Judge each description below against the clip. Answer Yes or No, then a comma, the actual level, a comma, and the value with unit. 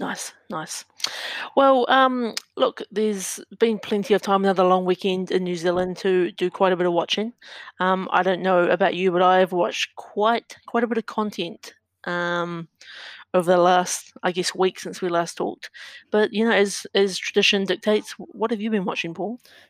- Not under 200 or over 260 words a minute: No, average, 190 wpm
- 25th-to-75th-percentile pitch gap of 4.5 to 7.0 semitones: No, average, 2.9 semitones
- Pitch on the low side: No, high, 190 Hz